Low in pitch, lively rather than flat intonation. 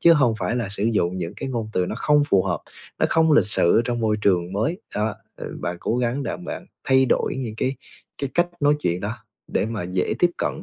Yes: low, 115 Hz; wide, 5.7 semitones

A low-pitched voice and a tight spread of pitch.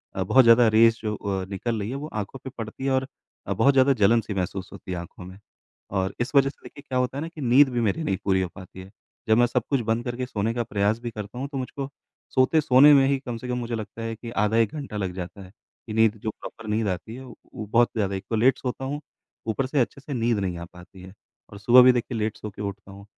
No: low, 115 Hz; average, 4.3 semitones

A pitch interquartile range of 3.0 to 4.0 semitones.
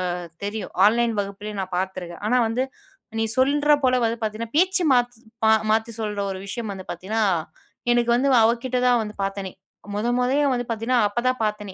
Yes: average, 3.3 semitones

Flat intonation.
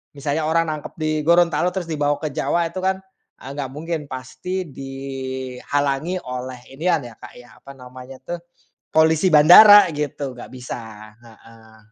No: average, 4.3 semitones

